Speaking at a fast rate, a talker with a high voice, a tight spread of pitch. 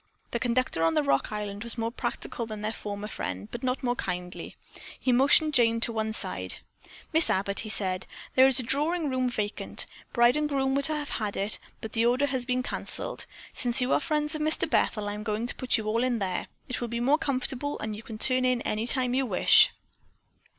No: fast, 220 wpm; high, 240 Hz; average, 3.7 semitones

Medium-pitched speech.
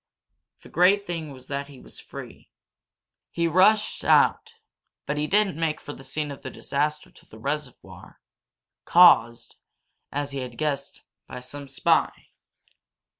Yes: medium, 150 Hz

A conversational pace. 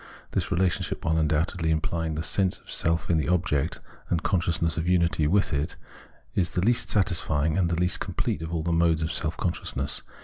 Yes: average, 195 wpm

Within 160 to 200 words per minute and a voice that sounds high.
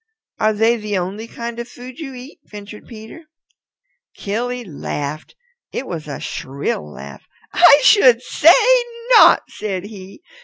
No: average, 140 wpm; high, 215 Hz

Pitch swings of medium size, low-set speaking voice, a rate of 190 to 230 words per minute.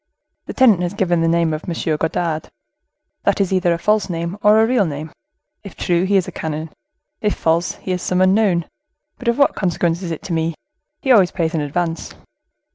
No: average, 3.2 semitones; medium, 175 Hz; fast, 205 wpm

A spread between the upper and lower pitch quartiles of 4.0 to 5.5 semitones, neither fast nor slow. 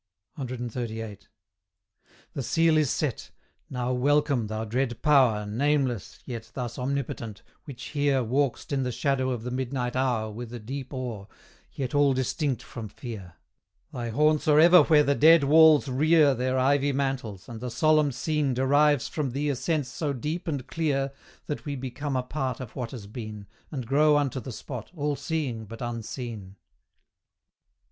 No: average, 3.4 semitones; average, 165 wpm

